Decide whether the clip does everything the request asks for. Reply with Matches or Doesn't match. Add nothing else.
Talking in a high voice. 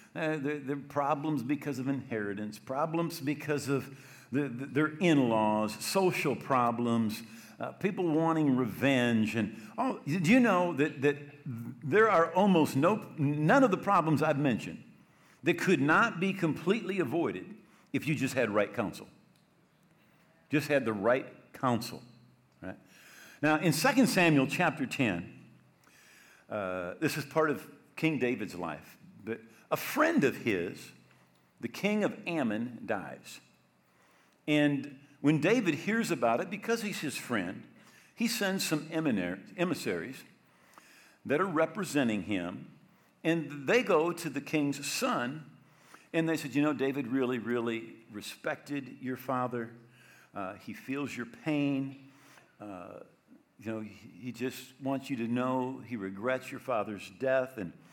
Doesn't match